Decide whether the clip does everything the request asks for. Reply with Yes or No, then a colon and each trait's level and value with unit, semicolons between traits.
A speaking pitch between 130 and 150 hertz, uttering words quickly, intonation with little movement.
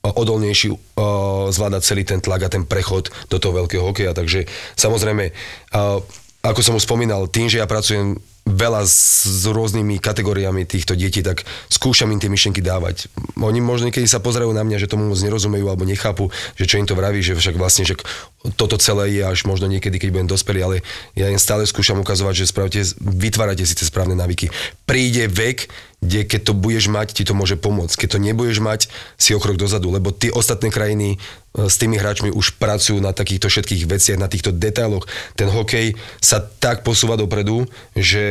No: low, 100 Hz; fast, 190 wpm; narrow, 2.1 semitones